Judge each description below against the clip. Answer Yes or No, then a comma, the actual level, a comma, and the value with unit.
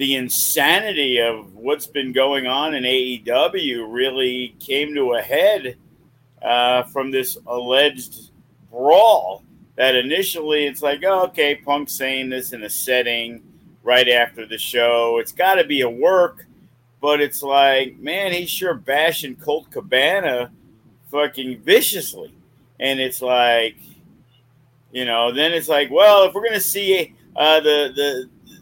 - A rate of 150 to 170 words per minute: No, average, 140 wpm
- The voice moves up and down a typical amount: Yes, average, 3.3 semitones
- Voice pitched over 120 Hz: Yes, low, 135 Hz